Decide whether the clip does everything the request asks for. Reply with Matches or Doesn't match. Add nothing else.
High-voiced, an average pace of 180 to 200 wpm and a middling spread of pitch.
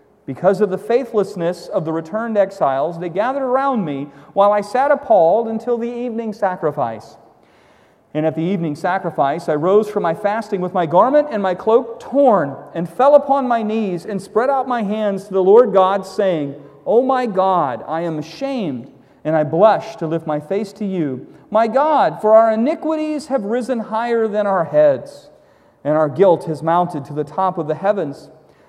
Doesn't match